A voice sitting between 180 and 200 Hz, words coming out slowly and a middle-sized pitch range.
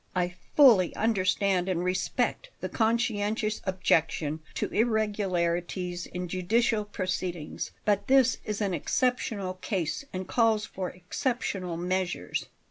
Yes: high, 190 Hz; slow, 115 wpm; average, 3.4 semitones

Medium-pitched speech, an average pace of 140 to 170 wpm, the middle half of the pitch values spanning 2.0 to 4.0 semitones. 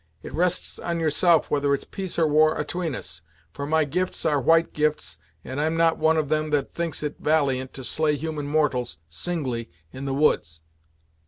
No: medium, 150 Hz; average, 185 wpm; average, 2.7 semitones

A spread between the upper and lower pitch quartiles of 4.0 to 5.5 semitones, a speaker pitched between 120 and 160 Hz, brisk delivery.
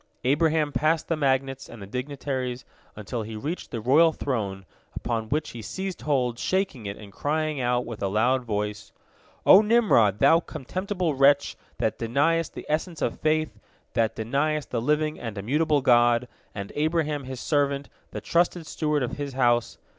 No: average, 4.6 semitones; medium, 140 Hz; average, 165 wpm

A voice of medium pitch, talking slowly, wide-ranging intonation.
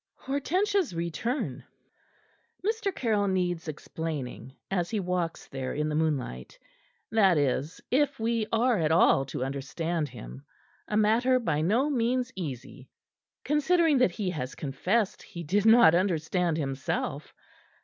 Yes: medium, 180 Hz; slow, 130 wpm; wide, 7.6 semitones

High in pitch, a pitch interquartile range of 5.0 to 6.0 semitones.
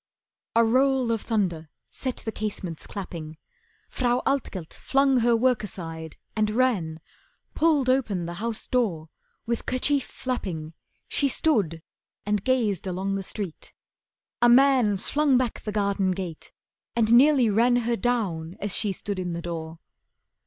Yes: high, 215 Hz; wide, 5.6 semitones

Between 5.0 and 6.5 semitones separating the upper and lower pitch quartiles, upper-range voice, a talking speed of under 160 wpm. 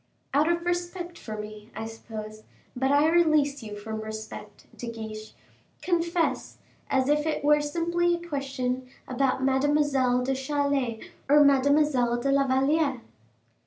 No: average, 4.0 semitones; very high, 275 Hz; average, 145 wpm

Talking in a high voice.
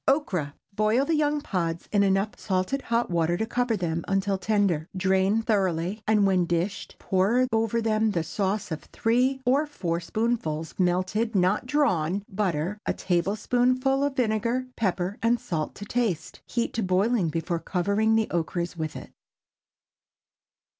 Yes: high, 200 Hz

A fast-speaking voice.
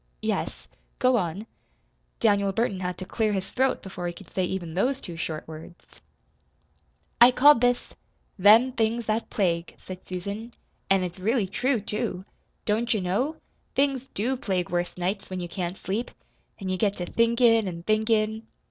No: average, 165 wpm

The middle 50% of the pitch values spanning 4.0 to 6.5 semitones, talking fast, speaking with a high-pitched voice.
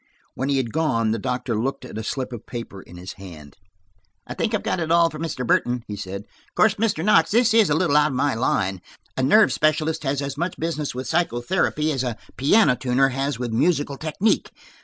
No: average, 5.2 semitones; fast, 220 wpm; medium, 140 Hz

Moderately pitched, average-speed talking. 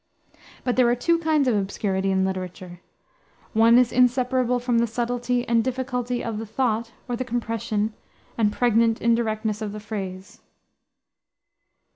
No: high, 230 Hz; average, 145 wpm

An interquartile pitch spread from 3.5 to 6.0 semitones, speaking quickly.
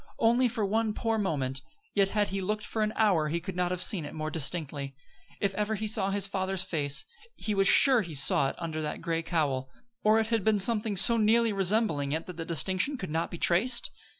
Yes: average, 4.9 semitones; fast, 230 wpm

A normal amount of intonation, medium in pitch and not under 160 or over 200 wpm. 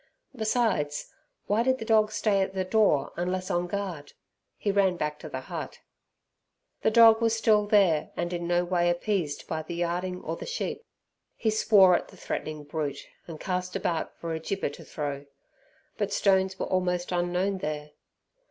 Yes: average, 3.7 semitones; medium, 180 Hz; average, 175 wpm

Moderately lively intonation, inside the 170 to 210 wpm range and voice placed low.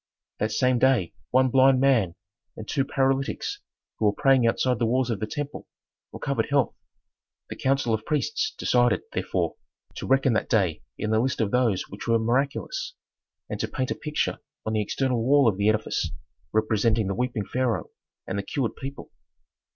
Yes: average, 3.5 semitones; average, 175 wpm; low, 120 Hz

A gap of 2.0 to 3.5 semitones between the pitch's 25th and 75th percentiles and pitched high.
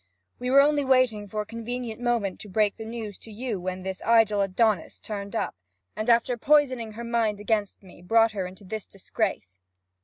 Yes: average, 2.8 semitones; high, 220 Hz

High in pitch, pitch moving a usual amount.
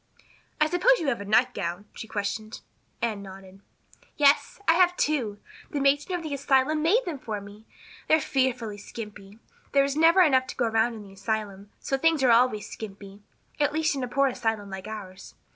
No: high, 240 Hz; wide, 6.0 semitones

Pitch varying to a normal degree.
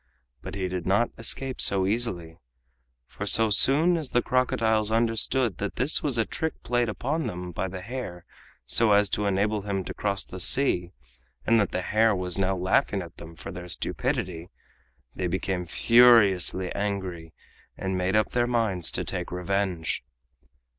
Yes: average, 4.2 semitones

